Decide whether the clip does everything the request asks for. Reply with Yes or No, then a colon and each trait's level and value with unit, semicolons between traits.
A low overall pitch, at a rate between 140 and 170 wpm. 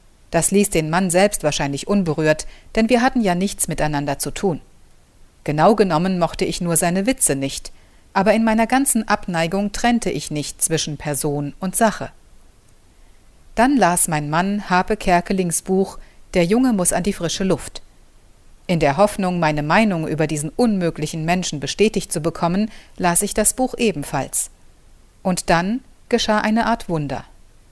No: medium, 175 Hz; average, 155 wpm